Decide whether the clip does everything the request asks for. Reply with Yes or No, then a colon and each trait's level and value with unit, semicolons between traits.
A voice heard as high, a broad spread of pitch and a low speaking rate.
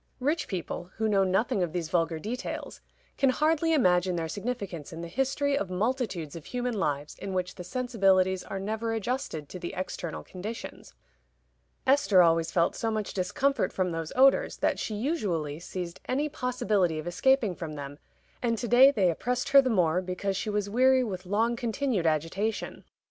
No: high, 200 Hz; wide, 6.0 semitones; average, 175 wpm